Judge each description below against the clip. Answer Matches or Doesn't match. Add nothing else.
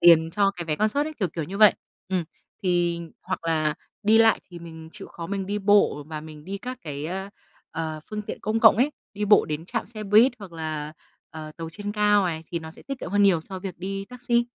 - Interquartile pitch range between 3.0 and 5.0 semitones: Matches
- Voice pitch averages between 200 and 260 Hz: Doesn't match